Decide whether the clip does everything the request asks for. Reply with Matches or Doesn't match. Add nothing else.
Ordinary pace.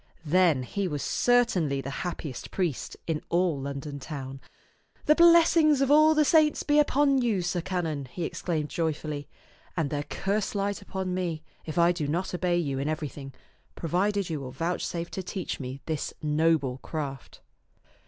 Matches